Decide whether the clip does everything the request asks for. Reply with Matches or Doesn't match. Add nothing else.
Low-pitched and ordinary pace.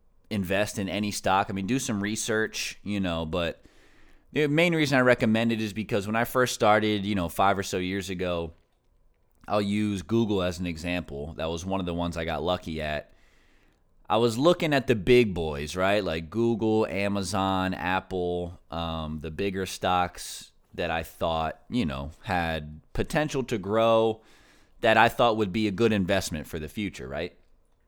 Matches